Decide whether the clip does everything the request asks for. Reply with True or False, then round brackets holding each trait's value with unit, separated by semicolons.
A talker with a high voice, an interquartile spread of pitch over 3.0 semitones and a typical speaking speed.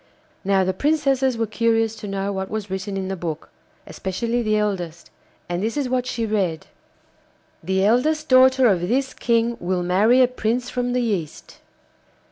True (220 Hz; 4.5 semitones; 170 wpm)